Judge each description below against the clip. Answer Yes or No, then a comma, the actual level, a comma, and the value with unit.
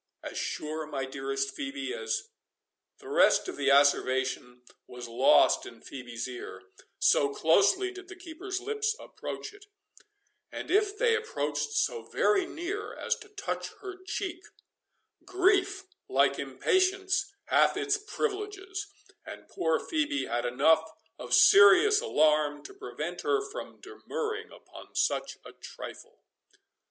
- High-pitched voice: Yes, very high, 375 Hz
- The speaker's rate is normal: No, slow, 130 wpm